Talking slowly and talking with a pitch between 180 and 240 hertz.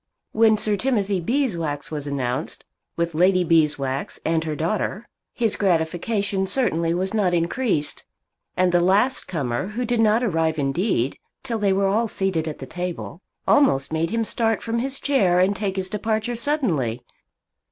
No: average, 160 wpm; high, 190 Hz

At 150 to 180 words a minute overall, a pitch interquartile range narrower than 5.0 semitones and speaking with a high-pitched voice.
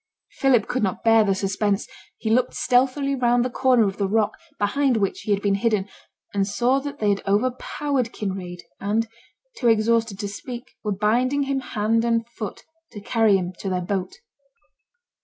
Yes: average, 175 wpm; average, 3.6 semitones; high, 225 Hz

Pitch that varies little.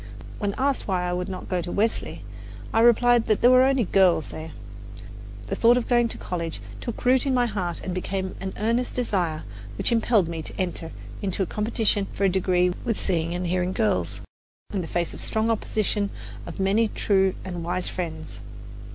No: average, 4.3 semitones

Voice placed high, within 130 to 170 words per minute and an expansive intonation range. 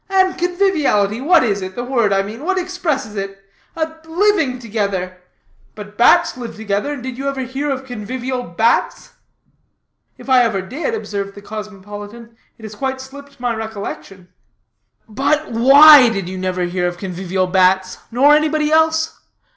Yes: high, 240 Hz; average, 160 wpm; wide, 6.5 semitones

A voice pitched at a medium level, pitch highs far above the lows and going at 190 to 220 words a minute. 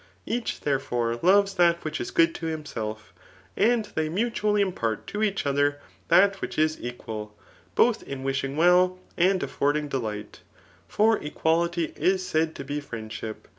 No: medium, 155 Hz; wide, 5.7 semitones; average, 150 wpm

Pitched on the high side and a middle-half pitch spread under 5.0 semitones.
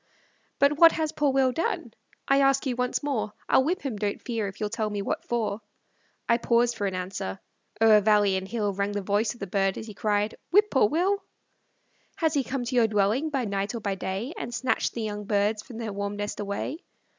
Yes: high, 220 Hz; average, 4.6 semitones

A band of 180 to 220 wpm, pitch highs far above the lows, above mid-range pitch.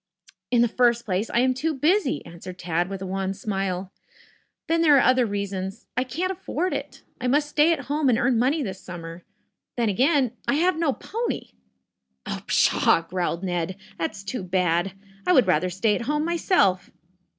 Yes: average, 185 wpm; wide, 7.7 semitones; high, 230 Hz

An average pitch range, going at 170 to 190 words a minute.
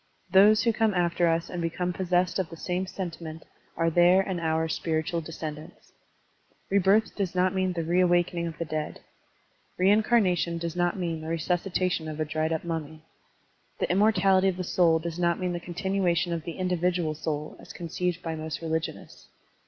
No: narrow, 2.2 semitones; average, 180 wpm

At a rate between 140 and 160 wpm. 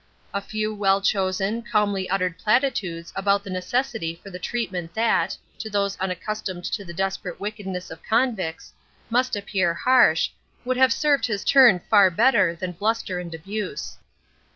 Yes: average, 150 wpm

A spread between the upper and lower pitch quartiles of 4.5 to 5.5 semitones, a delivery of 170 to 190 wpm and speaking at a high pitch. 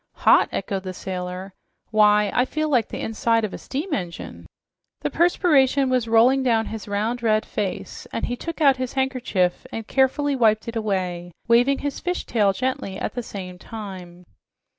Yes: average, 5.1 semitones; average, 175 wpm; high, 225 Hz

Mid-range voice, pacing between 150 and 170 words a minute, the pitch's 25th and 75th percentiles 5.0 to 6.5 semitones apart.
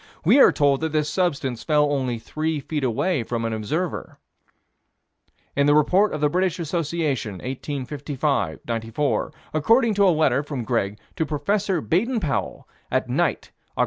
No: medium, 150 Hz; average, 155 wpm; average, 4.5 semitones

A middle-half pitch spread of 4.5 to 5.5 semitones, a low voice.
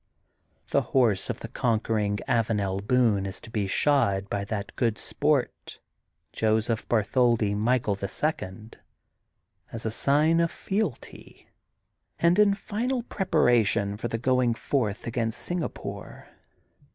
Yes: average, 4.9 semitones; low, 115 Hz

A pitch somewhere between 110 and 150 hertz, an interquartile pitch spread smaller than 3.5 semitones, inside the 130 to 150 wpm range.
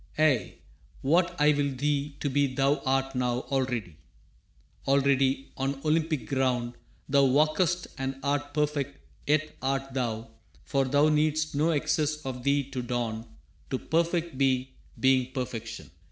Yes: low, 135 Hz; narrow, 2.5 semitones; average, 140 wpm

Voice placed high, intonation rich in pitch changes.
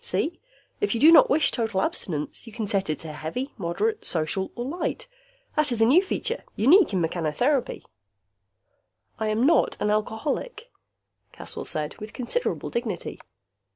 Yes: high, 230 Hz; wide, 8.0 semitones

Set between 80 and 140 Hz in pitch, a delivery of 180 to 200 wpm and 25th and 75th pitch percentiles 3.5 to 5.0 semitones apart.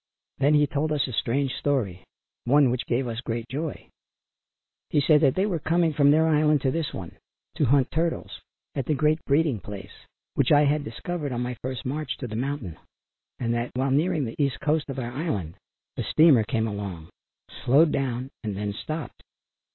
Yes: low, 135 Hz; average, 190 wpm; average, 4.3 semitones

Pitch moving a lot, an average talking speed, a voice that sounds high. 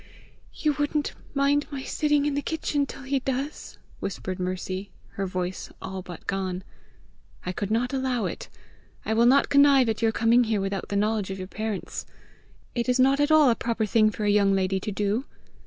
Yes: wide, 6.0 semitones; average, 195 wpm; high, 225 Hz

